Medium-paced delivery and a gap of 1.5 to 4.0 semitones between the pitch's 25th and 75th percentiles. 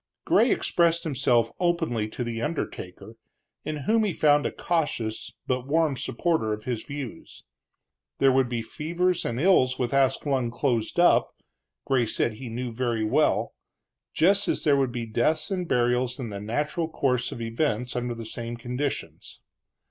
No: average, 160 wpm; average, 4.7 semitones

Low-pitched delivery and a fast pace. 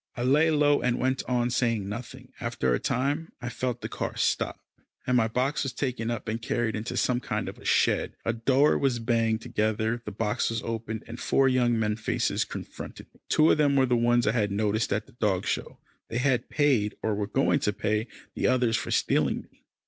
Yes: low, 120 Hz; fast, 220 wpm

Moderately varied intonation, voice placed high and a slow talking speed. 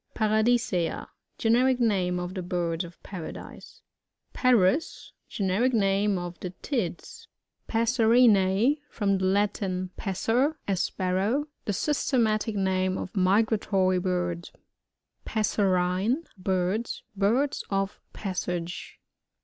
Yes: average, 3.6 semitones; high, 195 Hz; slow, 115 wpm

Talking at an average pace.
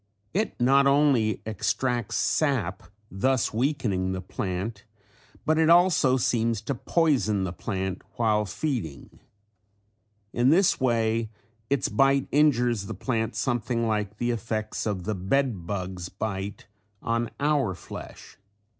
No: slow, 125 wpm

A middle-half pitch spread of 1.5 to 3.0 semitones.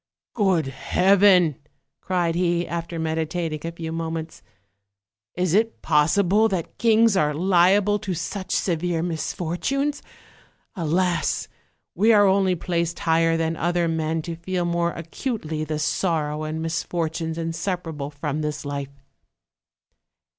Yes: narrow, 2.5 semitones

